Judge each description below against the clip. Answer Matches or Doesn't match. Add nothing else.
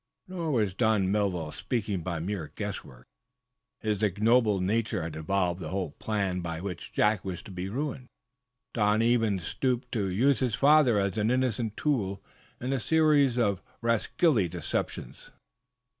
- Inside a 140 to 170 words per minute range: Matches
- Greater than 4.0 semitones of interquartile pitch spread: Matches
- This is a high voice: Doesn't match